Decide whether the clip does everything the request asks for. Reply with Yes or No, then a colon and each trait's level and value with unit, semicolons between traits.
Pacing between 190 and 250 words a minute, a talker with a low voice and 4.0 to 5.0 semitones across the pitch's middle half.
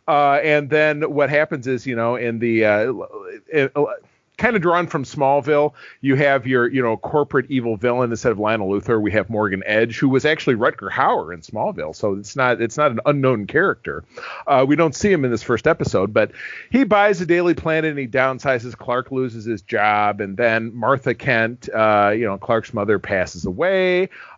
Yes: average, 200 wpm; low, 130 Hz; average, 4.7 semitones